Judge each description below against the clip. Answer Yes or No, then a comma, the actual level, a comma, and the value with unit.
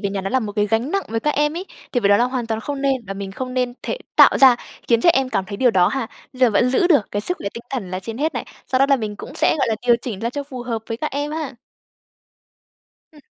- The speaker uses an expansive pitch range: No, average, 4.1 semitones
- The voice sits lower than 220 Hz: No, high, 245 Hz